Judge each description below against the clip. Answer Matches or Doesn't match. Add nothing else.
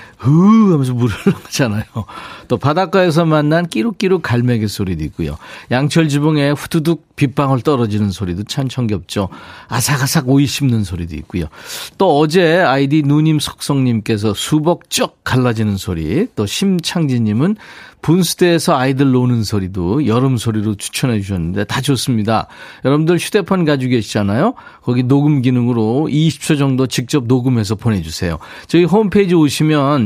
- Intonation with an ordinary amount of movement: Doesn't match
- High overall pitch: Doesn't match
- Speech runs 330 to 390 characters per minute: Matches